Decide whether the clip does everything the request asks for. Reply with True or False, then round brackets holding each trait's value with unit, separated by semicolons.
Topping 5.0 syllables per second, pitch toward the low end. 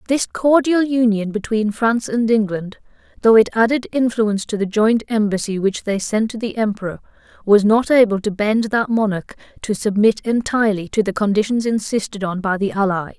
False (5.3 syllables/s; 215 Hz)